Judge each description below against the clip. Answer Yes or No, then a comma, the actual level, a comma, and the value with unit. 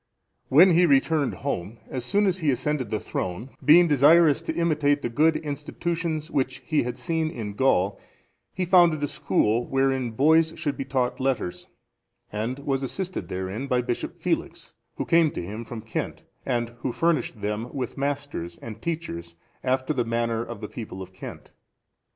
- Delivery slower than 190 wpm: Yes, average, 170 wpm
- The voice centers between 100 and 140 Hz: Yes, low, 135 Hz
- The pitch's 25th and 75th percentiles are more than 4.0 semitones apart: Yes, average, 5.2 semitones